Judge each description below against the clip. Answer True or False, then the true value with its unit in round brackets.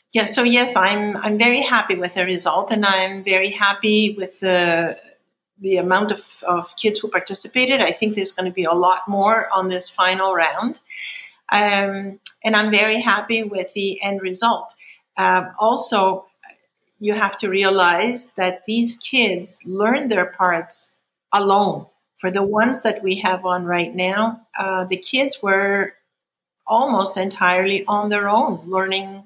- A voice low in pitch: False (195 Hz)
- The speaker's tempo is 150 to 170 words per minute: True (160 wpm)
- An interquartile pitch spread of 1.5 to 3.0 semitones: True (2.5 semitones)